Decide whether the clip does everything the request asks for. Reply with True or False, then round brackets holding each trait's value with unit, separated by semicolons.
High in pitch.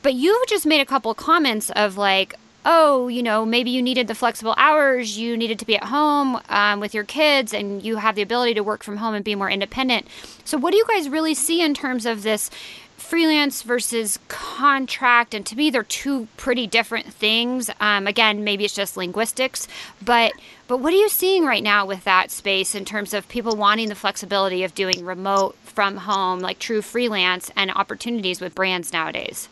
True (225 Hz)